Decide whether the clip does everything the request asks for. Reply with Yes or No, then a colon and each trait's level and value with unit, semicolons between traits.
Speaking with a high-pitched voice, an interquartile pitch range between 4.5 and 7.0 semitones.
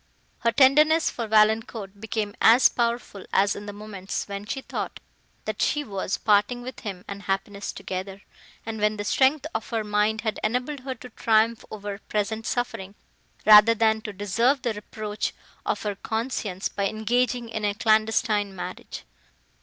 No: high, 215 Hz; narrow, 2.4 semitones